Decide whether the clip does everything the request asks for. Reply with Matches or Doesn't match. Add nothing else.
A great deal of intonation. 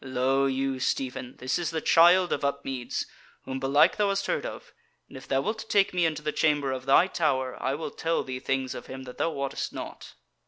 Doesn't match